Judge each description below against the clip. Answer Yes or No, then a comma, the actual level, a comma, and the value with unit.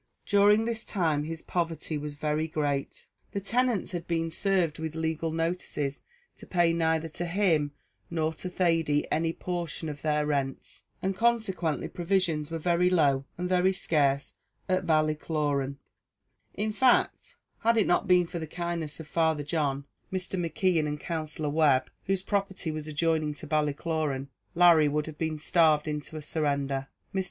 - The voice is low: No, medium, 160 Hz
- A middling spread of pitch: Yes, average, 3.0 semitones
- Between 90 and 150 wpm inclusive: No, average, 160 wpm